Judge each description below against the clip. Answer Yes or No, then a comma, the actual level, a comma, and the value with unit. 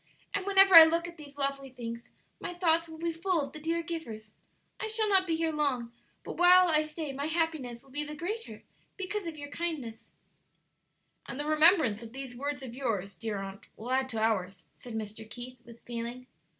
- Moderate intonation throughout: No, wide, 5.9 semitones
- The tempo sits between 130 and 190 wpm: No, fast, 205 wpm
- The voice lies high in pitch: Yes, very high, 290 Hz